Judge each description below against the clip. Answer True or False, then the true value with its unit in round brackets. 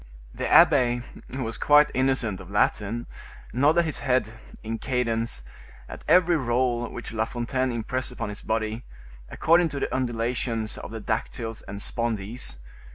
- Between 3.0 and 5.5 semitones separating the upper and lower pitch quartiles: False (2.6 semitones)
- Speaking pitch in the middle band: False (120 Hz)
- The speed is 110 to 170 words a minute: True (150 wpm)